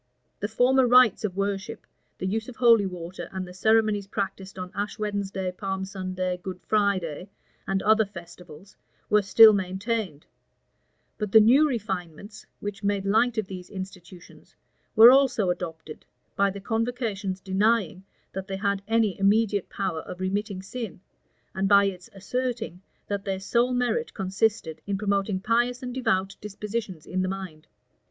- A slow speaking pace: No, average, 150 wpm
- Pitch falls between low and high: No, high, 200 Hz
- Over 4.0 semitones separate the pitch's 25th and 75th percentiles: No, average, 2.9 semitones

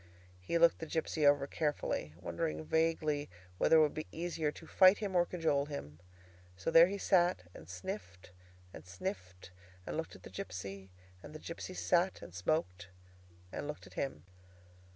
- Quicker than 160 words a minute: Yes, average, 170 wpm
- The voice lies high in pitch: No, medium, 150 Hz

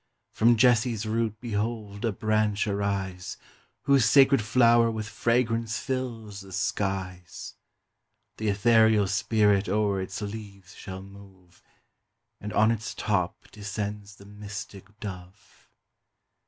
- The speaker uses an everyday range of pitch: No, narrow, 2.3 semitones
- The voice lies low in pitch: Yes, low, 105 Hz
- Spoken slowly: Yes, slow, 115 wpm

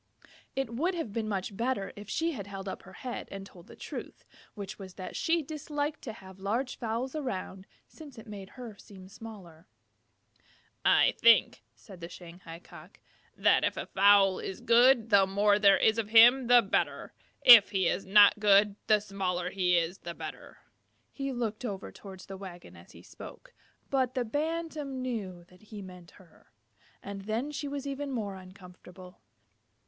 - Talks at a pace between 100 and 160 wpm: No, average, 175 wpm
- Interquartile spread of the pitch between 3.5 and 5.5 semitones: Yes, average, 4.8 semitones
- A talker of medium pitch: No, high, 205 Hz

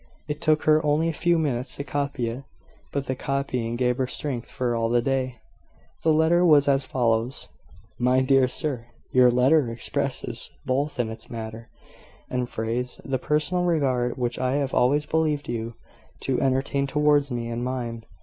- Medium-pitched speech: No, low, 130 Hz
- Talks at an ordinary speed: Yes, average, 170 wpm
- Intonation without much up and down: No, average, 3.2 semitones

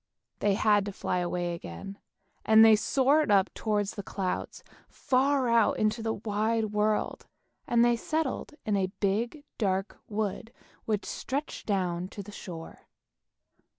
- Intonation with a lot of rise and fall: No, average, 2.9 semitones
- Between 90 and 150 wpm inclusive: Yes, average, 145 wpm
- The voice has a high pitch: Yes, high, 210 Hz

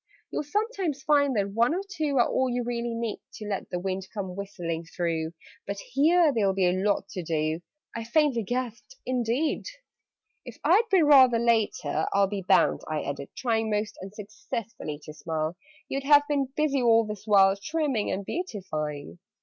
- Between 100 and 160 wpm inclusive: No, average, 175 wpm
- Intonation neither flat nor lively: No, wide, 6.2 semitones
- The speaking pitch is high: Yes, high, 225 Hz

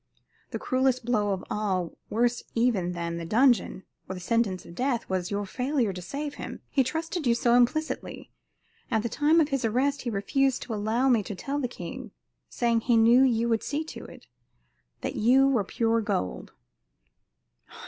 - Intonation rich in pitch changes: No, average, 4.5 semitones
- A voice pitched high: Yes, high, 235 Hz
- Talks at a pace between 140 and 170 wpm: No, average, 180 wpm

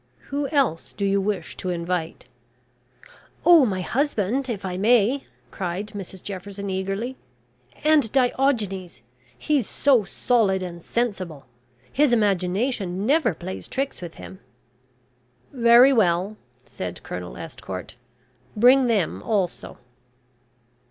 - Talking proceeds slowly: Yes, slow, 110 wpm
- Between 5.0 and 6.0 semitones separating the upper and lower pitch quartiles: Yes, average, 5.3 semitones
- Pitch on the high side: Yes, high, 205 Hz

